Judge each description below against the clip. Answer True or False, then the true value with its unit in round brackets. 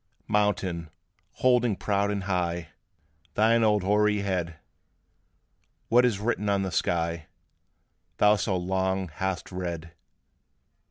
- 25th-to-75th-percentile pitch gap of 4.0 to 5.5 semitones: False (2.9 semitones)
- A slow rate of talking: True (110 wpm)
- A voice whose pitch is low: True (95 Hz)